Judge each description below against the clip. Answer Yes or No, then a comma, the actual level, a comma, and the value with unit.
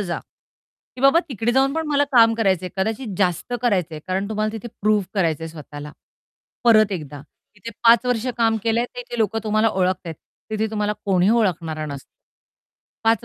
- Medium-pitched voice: No, high, 215 Hz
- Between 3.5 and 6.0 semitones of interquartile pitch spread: Yes, average, 4.1 semitones